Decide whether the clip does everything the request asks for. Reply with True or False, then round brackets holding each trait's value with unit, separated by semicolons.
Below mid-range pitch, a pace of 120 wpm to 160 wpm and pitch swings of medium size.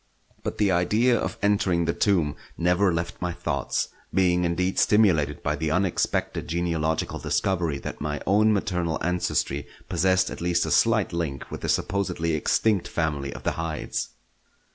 True (85 Hz; 155 wpm; 3.0 semitones)